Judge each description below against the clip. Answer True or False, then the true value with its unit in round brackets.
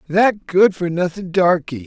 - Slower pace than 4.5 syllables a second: True (4.1 syllables/s)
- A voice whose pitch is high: False (180 Hz)